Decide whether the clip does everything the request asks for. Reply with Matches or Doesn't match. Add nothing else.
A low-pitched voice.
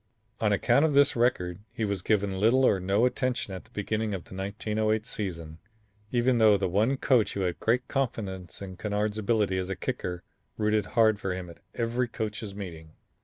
Matches